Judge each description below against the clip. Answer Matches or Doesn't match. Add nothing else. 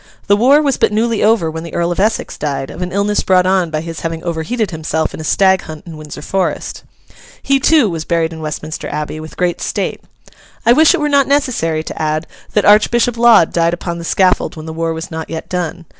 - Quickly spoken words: Matches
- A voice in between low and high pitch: Matches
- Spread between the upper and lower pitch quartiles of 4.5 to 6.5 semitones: Matches